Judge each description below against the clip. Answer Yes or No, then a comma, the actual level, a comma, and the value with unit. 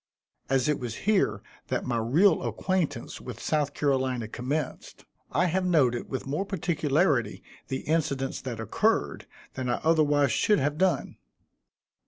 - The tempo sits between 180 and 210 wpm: No, average, 140 wpm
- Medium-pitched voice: Yes, medium, 145 Hz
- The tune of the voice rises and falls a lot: No, average, 4.3 semitones